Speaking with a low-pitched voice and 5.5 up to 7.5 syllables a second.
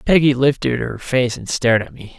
No: low, 125 Hz; 5.3 syllables/s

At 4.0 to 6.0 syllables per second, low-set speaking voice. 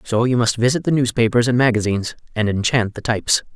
No: 6.3 syllables/s; low, 115 Hz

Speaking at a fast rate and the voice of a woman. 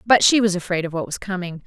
Yes: fast, 290 wpm; female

